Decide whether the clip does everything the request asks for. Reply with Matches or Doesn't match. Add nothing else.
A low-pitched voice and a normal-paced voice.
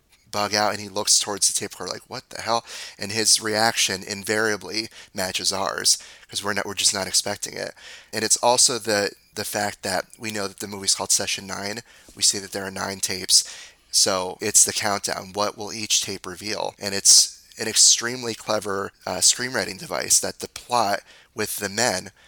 Matches